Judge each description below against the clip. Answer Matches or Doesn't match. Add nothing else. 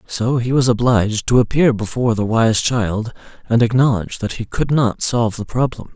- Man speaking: Matches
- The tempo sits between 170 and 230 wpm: Matches